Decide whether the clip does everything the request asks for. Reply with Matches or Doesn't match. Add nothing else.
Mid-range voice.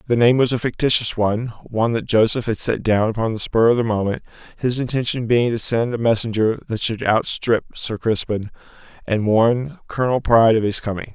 Doesn't match